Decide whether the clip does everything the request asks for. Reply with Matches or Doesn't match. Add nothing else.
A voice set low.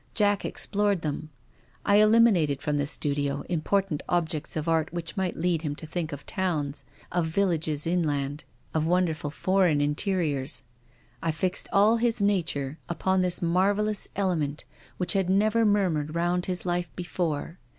Doesn't match